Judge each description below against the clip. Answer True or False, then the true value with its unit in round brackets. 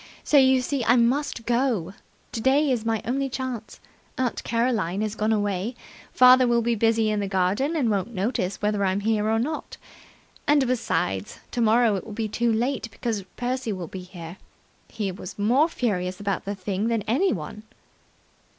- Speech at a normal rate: True (170 wpm)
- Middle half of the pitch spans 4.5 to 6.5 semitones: False (3.8 semitones)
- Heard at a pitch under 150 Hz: False (225 Hz)